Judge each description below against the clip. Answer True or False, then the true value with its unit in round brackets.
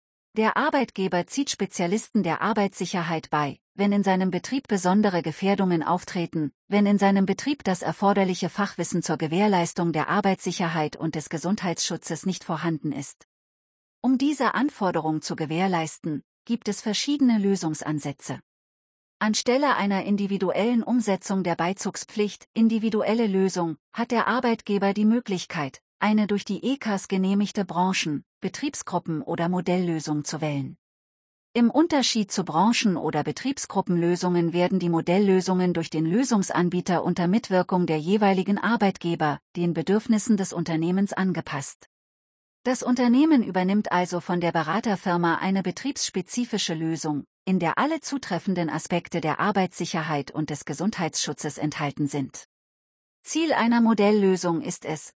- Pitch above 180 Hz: True (190 Hz)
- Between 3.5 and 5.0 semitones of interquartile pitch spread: True (4.0 semitones)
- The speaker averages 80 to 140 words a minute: True (125 wpm)